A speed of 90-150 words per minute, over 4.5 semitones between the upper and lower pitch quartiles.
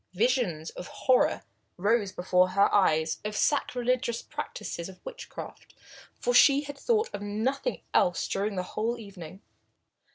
Yes: average, 140 wpm; wide, 5.5 semitones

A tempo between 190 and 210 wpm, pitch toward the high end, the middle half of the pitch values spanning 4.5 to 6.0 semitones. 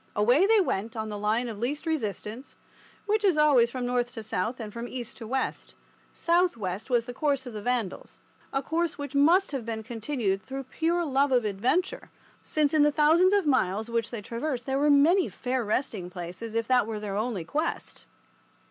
Yes: average, 195 wpm; very high, 250 Hz; average, 5.2 semitones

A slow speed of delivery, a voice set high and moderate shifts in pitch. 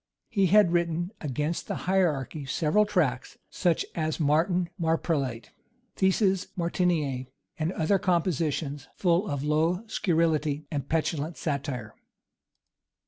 No: slow, 110 wpm; medium, 165 Hz; average, 3.3 semitones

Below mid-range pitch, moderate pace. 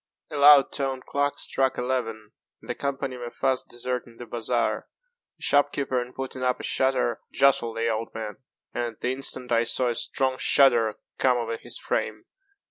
Yes: low, 125 Hz; average, 185 wpm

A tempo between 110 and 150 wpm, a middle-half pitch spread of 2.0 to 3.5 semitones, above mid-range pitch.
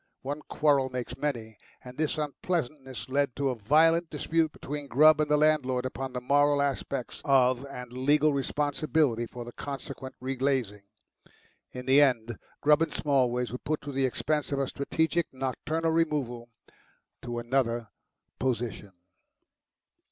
No: average, 145 wpm; average, 3.0 semitones; low, 135 Hz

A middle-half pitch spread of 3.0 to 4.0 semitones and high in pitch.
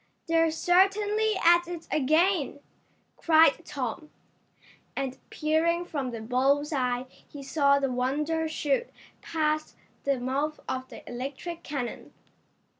Yes: average, 3.7 semitones; very high, 300 Hz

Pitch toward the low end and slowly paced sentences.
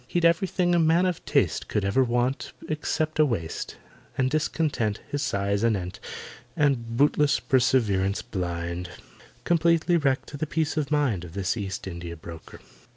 No: low, 130 Hz; average, 150 wpm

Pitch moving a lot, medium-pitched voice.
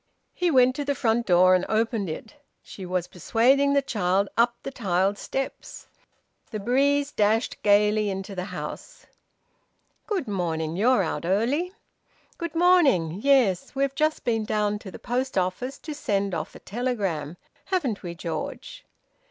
No: wide, 6.3 semitones; high, 220 Hz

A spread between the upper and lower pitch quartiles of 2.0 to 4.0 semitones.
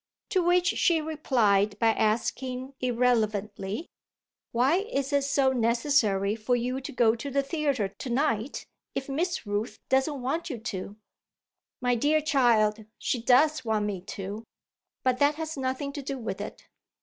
No: average, 4.6 semitones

